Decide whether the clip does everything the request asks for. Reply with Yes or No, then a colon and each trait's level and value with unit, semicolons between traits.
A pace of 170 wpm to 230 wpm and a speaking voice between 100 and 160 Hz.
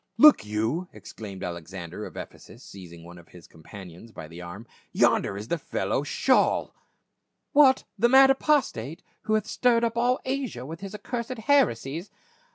Yes: average, 175 wpm; low, 135 Hz